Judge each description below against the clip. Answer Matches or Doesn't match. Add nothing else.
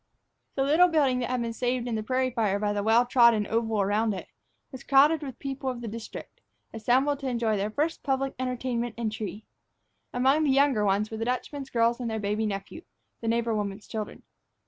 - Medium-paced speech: Doesn't match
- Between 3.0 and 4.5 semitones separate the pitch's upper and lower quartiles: Matches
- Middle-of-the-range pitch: Doesn't match